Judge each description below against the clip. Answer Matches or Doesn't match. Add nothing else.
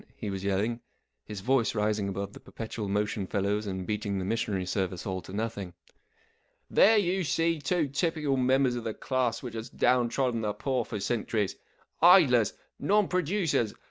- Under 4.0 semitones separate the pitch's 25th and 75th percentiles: Doesn't match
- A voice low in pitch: Matches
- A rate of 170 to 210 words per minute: Matches